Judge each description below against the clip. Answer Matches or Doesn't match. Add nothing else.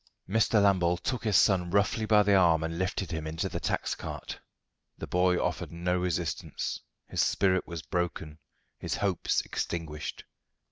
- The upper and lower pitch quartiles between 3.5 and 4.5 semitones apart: Doesn't match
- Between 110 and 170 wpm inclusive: Matches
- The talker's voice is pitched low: Matches